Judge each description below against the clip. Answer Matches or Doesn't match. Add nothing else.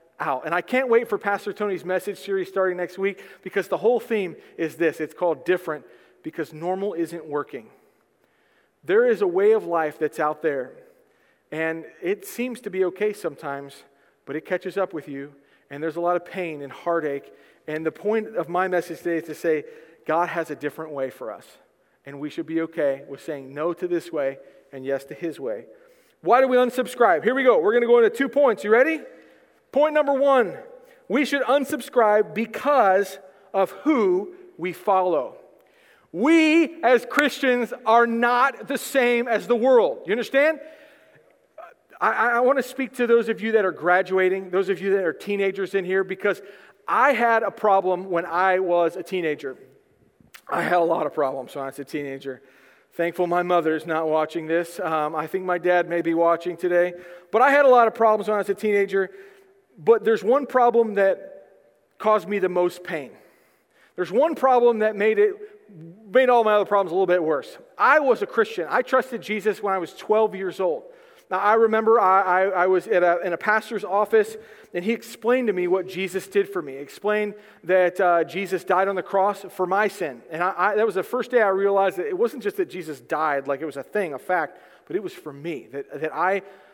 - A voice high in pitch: Matches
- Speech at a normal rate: Doesn't match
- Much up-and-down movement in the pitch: Matches